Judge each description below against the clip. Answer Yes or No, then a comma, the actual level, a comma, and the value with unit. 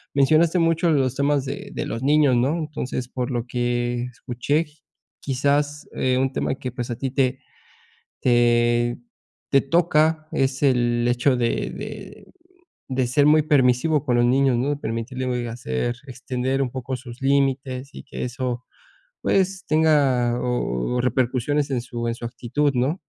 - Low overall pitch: Yes, low, 130 Hz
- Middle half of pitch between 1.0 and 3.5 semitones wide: Yes, average, 2.9 semitones